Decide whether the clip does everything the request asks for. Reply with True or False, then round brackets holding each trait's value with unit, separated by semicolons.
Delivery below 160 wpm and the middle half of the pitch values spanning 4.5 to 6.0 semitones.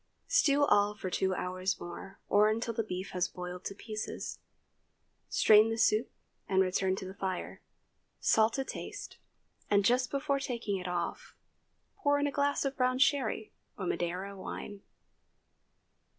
True (150 wpm; 5.2 semitones)